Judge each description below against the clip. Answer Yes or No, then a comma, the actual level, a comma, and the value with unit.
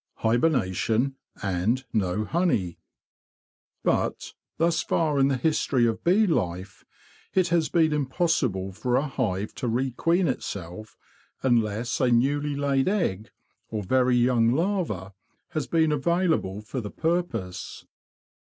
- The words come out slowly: Yes, slow, 125 wpm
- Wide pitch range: Yes, wide, 6.9 semitones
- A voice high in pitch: No, low, 130 Hz